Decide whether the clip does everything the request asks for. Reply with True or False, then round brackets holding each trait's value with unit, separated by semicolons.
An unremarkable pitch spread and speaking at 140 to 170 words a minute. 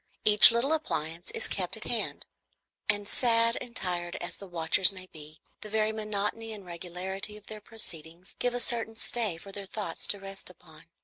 False (4.1 semitones; 185 wpm)